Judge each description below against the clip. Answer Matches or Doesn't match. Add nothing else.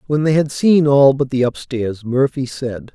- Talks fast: Matches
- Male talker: Matches